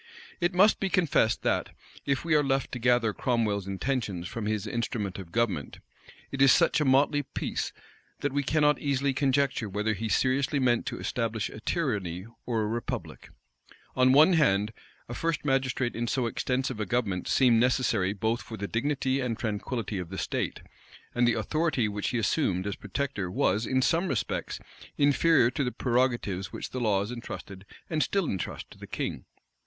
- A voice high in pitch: No, low, 120 Hz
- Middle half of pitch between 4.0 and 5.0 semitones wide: Yes, average, 4.7 semitones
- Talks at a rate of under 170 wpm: No, average, 180 wpm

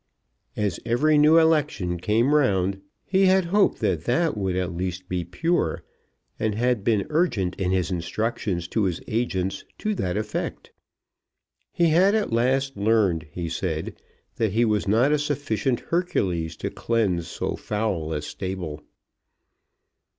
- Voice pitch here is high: No, low, 105 Hz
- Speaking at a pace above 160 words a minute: No, average, 145 wpm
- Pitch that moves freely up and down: Yes, wide, 7.3 semitones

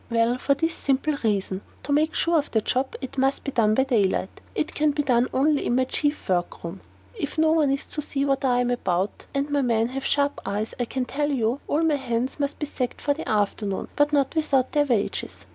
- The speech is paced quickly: Yes, fast, 235 wpm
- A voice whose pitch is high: Yes, very high, 265 Hz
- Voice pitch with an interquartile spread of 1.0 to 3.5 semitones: No, average, 4.0 semitones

